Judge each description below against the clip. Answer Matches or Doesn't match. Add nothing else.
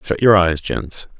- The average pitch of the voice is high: Doesn't match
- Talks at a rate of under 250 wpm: Matches